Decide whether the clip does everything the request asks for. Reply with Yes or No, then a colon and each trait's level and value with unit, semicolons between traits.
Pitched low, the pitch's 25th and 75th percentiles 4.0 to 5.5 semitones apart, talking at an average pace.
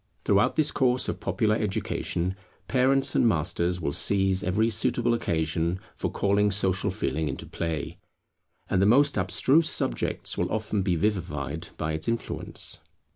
Yes: very low, 95 Hz; average, 5.0 semitones; average, 145 wpm